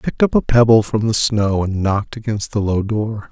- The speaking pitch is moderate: No, low, 110 Hz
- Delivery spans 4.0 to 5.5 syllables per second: No, 5.7 syllables/s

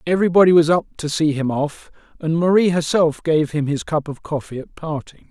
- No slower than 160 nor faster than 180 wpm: No, fast, 205 wpm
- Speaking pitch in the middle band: Yes, medium, 155 Hz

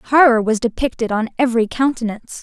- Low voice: No, high, 240 Hz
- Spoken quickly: No, average, 150 wpm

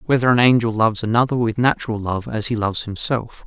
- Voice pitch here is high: No, low, 115 Hz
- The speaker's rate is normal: No, fast, 210 wpm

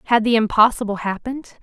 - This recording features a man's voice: No, female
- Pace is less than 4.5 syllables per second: No, 6.3 syllables/s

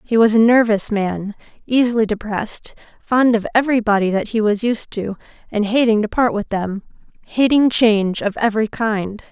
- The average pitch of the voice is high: Yes, high, 220 Hz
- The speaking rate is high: No, average, 175 wpm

